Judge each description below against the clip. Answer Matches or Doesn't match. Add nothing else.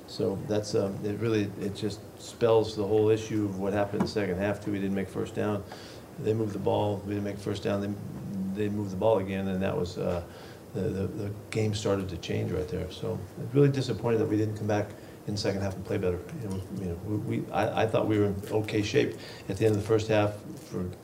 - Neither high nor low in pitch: Doesn't match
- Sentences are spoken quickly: Matches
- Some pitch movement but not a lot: Doesn't match